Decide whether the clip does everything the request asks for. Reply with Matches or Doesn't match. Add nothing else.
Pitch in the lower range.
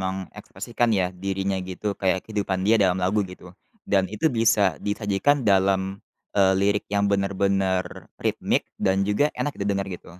Matches